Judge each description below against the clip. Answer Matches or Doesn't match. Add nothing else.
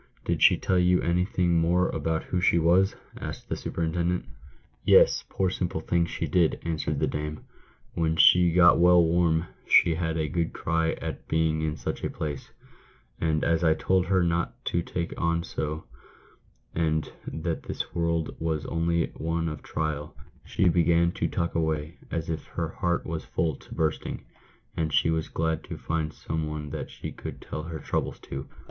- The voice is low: Matches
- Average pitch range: Doesn't match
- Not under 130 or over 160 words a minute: Doesn't match